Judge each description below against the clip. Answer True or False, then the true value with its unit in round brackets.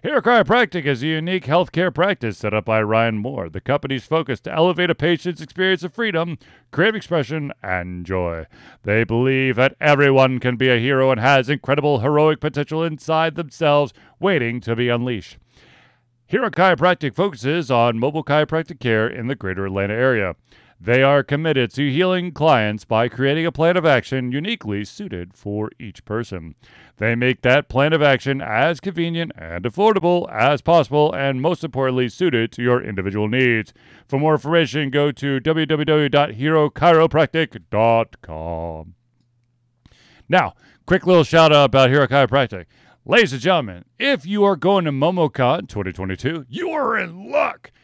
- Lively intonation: True (5.7 semitones)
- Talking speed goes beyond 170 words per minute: False (155 wpm)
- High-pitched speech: False (140 Hz)